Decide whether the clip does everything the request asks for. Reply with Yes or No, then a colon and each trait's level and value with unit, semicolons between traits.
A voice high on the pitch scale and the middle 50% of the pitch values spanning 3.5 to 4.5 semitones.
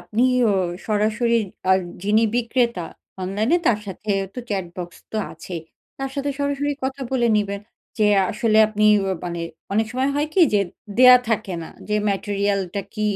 Yes: high, 215 Hz; average, 3.9 semitones